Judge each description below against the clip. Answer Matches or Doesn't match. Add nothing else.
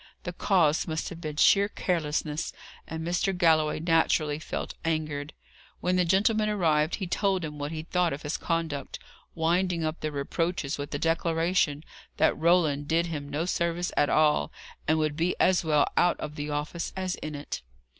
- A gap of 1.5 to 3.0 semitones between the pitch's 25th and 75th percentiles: Matches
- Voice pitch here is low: Doesn't match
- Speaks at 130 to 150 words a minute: Doesn't match